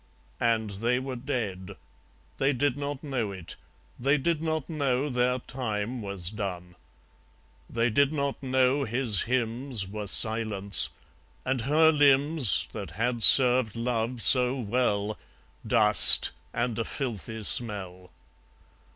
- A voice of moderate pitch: No, low, 120 Hz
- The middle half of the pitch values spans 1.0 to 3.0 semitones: No, average, 4.0 semitones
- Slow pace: Yes, slow, 125 wpm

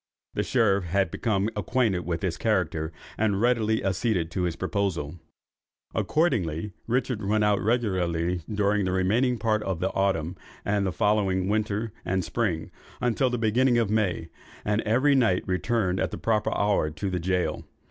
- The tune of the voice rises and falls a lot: No, average, 3.5 semitones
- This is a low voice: Yes, low, 100 Hz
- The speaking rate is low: No, average, 160 wpm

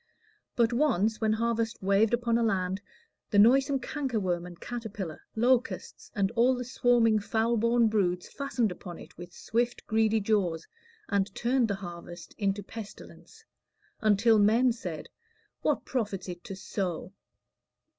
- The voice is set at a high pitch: Yes, high, 220 Hz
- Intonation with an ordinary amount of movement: Yes, average, 3.4 semitones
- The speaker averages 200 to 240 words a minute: No, average, 140 wpm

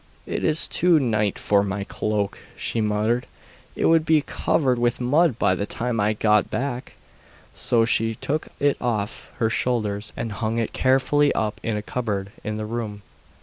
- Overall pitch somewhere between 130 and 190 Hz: No, low, 115 Hz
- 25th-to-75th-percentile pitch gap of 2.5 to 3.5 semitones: Yes, average, 3.1 semitones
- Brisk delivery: No, average, 175 wpm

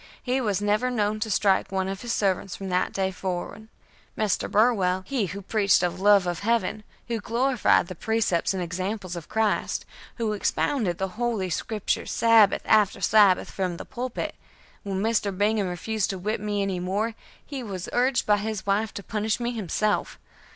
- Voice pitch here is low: No, high, 205 Hz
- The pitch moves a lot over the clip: No, average, 2.7 semitones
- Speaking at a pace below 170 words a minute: No, average, 175 wpm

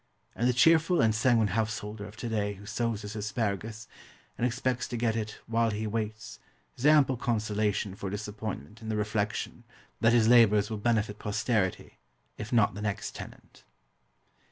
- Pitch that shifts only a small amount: Yes, narrow, 2.0 semitones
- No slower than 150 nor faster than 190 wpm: Yes, average, 165 wpm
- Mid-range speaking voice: No, low, 110 Hz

